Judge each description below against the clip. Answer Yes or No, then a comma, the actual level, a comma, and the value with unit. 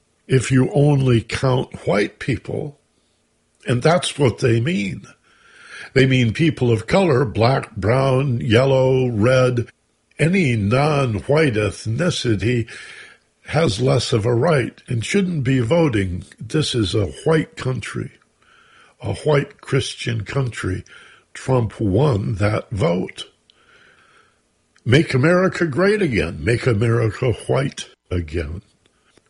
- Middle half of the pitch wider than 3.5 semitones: Yes, average, 4.4 semitones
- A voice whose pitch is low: Yes, low, 130 Hz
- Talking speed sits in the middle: No, slow, 110 wpm